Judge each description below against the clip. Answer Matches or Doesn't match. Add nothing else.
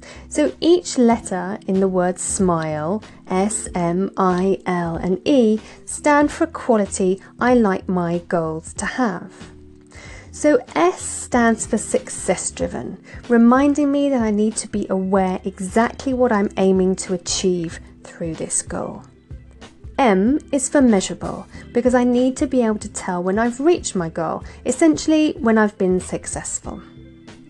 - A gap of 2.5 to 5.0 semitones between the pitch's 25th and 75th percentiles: Doesn't match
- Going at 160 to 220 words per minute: Doesn't match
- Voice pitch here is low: Doesn't match